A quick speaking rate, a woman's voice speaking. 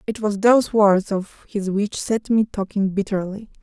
No: average, 180 wpm; female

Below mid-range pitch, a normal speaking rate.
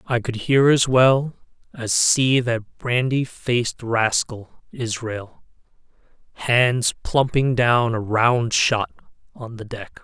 No: low, 120 Hz; slow, 125 wpm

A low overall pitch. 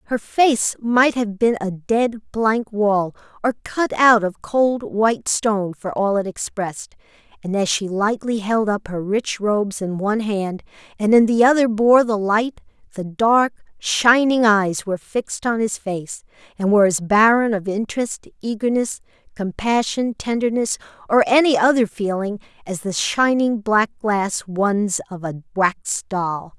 No: high, 215 Hz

